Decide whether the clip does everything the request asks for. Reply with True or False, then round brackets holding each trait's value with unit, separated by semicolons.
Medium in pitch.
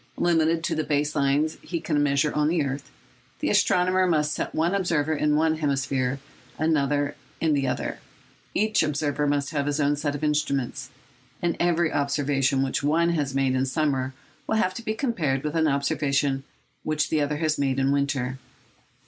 True (145 Hz)